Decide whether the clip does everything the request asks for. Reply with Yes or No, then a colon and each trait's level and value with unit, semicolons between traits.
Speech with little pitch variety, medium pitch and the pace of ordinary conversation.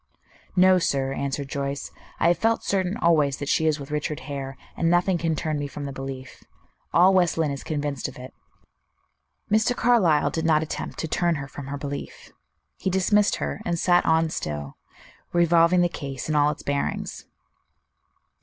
No: average, 3.8 semitones; medium, 155 Hz; average, 180 wpm